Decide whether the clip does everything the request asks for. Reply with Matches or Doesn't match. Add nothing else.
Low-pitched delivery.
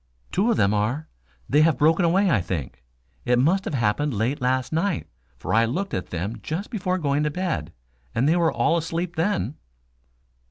Doesn't match